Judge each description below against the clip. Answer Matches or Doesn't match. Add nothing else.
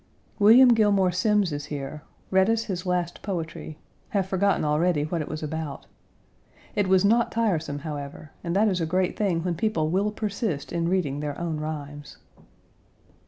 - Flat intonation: Doesn't match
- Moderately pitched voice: Matches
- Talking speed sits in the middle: Matches